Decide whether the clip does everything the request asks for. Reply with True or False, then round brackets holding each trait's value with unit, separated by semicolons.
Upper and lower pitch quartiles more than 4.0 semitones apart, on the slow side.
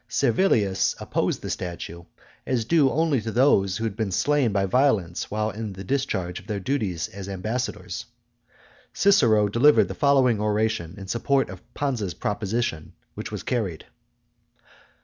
False (5.2 semitones; 145 wpm)